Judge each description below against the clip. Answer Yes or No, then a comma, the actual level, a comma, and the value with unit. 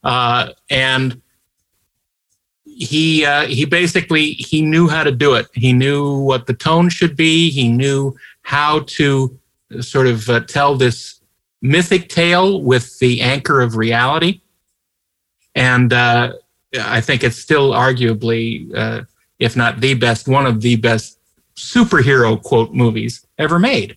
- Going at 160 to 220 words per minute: No, average, 140 wpm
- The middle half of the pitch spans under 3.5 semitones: No, average, 4.4 semitones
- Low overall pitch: Yes, low, 130 Hz